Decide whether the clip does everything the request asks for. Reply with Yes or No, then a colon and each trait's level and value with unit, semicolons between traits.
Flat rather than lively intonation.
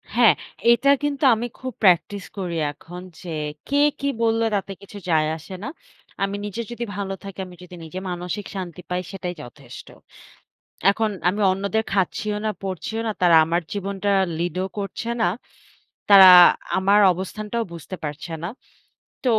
No: average, 3.1 semitones